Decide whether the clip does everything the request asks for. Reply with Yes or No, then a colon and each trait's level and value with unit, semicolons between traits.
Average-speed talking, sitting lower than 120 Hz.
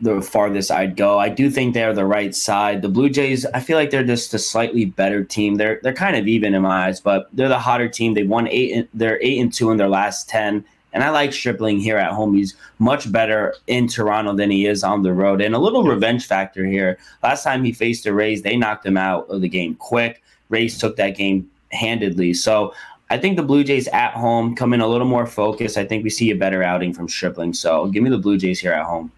No: fast, 255 wpm; low, 110 Hz